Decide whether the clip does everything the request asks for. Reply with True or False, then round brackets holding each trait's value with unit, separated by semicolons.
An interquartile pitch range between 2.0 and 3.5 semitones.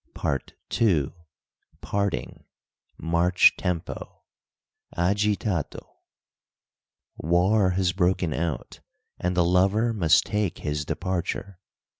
True (2.8 semitones)